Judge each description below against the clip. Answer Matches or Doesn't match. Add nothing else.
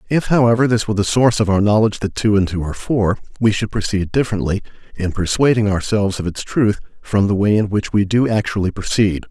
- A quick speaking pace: Matches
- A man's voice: Matches